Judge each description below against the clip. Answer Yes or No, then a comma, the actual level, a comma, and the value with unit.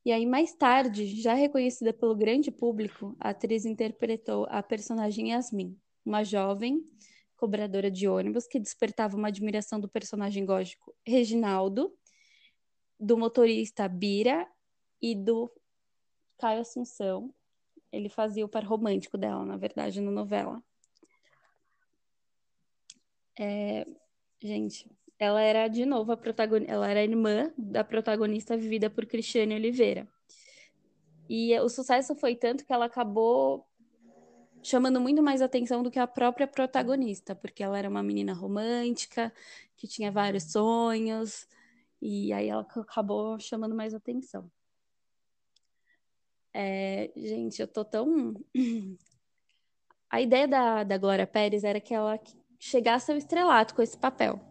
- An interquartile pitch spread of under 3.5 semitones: Yes, average, 3.0 semitones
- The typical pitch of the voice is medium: No, high, 225 Hz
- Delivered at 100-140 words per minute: Yes, average, 130 wpm